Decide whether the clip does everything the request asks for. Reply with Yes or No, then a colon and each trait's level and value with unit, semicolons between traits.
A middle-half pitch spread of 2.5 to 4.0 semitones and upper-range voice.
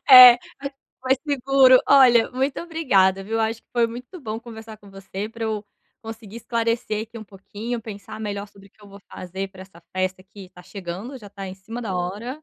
Yes: average, 3.7 semitones; high, 220 Hz